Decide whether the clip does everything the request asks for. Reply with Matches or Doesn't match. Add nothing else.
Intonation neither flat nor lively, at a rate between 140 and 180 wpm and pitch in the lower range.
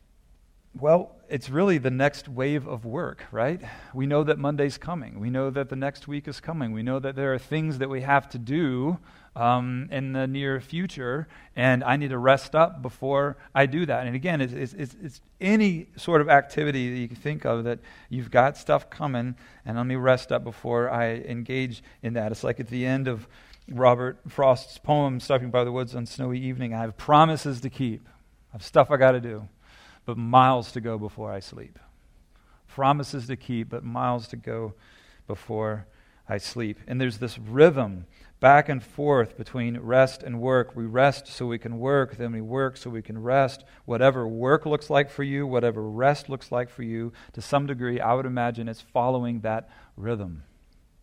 Doesn't match